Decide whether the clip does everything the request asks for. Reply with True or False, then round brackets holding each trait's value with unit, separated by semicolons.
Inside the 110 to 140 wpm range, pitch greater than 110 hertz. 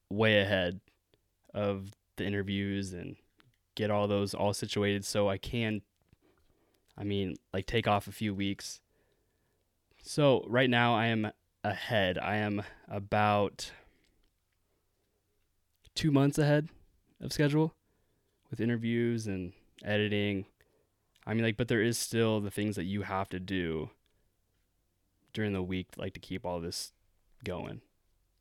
False (135 wpm; 100 Hz)